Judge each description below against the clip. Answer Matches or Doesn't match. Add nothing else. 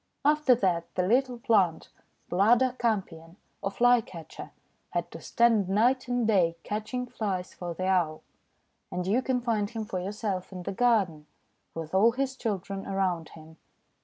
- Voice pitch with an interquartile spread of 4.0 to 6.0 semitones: Matches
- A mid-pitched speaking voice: Doesn't match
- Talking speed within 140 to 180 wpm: Matches